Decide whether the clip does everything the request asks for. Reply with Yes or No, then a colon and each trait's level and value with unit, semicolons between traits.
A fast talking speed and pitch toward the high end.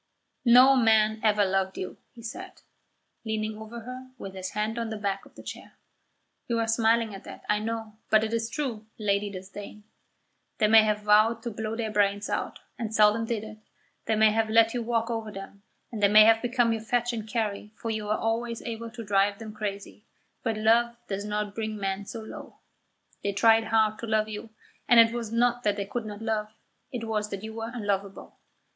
Yes: fast, 210 wpm; high, 220 Hz